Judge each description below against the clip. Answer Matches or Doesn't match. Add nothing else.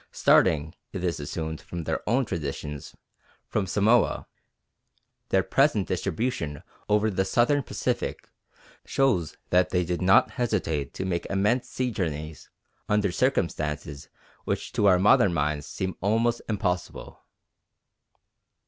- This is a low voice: Matches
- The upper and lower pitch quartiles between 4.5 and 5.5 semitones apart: Matches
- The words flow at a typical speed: Doesn't match